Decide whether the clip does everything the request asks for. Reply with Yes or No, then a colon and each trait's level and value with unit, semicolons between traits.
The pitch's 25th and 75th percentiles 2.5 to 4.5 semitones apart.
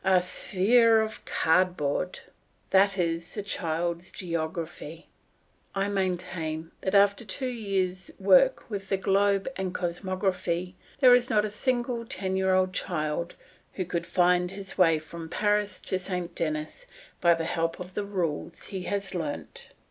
Yes: average, 2.8 semitones